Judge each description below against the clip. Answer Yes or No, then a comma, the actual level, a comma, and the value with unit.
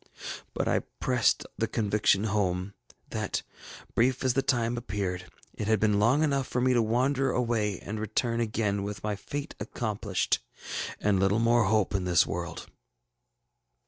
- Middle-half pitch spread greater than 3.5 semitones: No, average, 3.1 semitones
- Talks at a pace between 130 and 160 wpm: Yes, average, 155 wpm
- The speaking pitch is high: No, low, 110 Hz